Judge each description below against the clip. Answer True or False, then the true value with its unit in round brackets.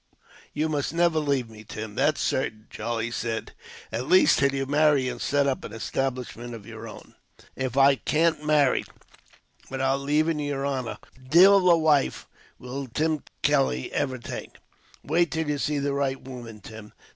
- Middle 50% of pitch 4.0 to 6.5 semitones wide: False (3.5 semitones)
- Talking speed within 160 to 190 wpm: True (165 wpm)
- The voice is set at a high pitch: False (140 Hz)